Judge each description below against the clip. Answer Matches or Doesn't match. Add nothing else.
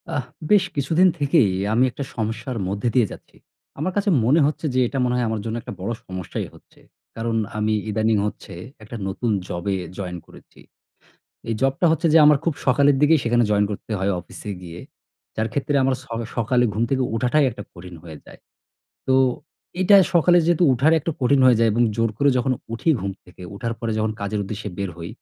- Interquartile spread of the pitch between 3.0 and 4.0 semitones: Doesn't match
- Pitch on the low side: Matches